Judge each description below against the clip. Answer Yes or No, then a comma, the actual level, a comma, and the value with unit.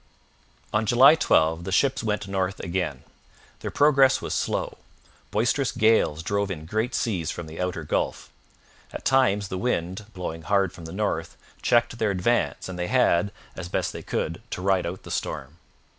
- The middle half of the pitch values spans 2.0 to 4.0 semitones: No, average, 4.7 semitones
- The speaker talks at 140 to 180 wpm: Yes, average, 175 wpm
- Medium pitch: No, very low, 95 Hz